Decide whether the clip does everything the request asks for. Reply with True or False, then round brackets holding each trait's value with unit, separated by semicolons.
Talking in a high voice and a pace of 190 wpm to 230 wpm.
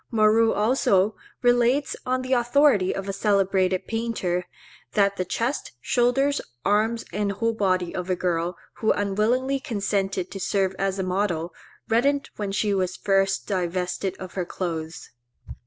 False (200 Hz; 145 wpm)